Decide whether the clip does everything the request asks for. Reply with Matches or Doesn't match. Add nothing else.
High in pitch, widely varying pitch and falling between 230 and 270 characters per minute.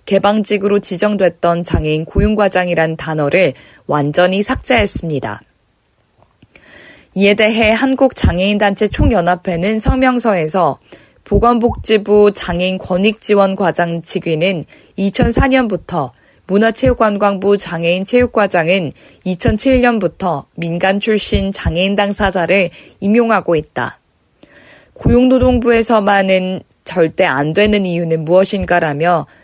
Doesn't match